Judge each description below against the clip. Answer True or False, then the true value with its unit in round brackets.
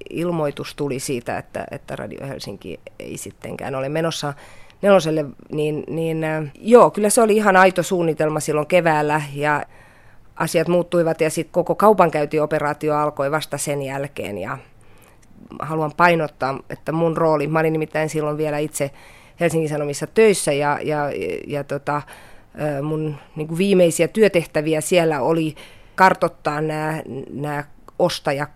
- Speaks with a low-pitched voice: False (155 Hz)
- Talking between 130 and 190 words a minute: True (135 wpm)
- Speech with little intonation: True (2.3 semitones)